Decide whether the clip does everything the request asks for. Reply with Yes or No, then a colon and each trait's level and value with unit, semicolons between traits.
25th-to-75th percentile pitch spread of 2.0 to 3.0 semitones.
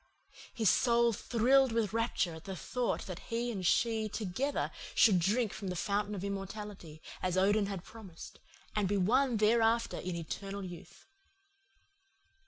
No: average, 3.6 semitones